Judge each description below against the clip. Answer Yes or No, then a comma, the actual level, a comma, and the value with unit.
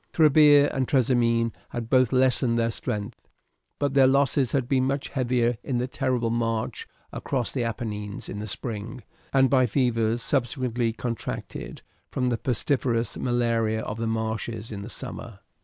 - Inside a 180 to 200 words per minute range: No, average, 155 wpm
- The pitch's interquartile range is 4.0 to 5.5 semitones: No, narrow, 2.5 semitones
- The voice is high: No, low, 120 Hz